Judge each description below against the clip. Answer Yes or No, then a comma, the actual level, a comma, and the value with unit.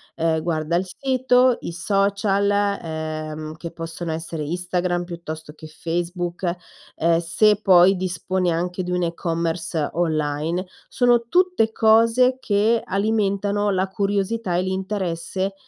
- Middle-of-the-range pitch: Yes, medium, 180 Hz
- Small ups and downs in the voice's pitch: No, average, 3.5 semitones